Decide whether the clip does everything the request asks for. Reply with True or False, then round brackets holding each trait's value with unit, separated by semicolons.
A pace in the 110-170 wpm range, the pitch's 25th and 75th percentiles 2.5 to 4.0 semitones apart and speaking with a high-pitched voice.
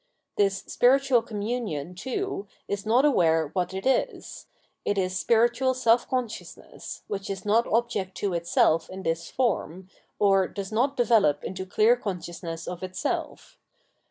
False (145 wpm; 4.6 semitones; 200 Hz)